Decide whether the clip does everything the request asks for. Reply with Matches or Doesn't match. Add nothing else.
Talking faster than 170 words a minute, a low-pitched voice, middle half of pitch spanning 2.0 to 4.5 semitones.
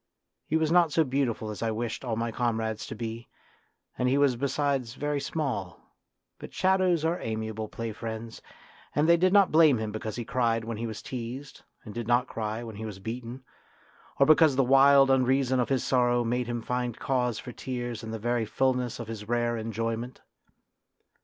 Matches